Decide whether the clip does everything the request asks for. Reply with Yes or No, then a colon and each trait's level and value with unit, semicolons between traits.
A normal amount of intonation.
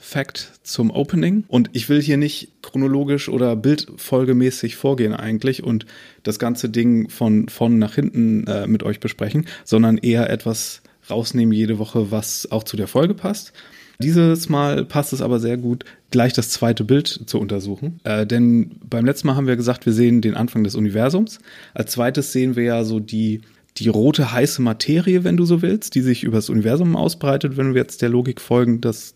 Yes: average, 4.2 semitones